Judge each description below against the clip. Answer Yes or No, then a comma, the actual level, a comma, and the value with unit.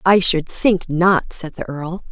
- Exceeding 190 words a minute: Yes, average, 200 wpm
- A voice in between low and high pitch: Yes, medium, 175 Hz